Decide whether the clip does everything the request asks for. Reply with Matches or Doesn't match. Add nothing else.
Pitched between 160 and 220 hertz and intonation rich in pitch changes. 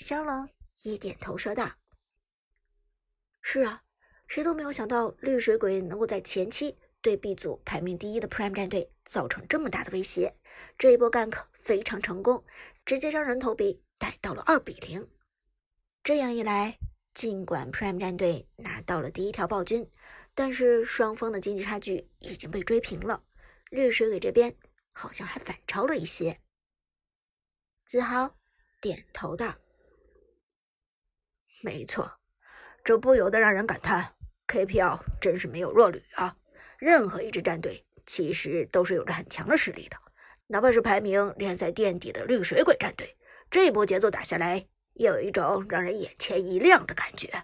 Doesn't match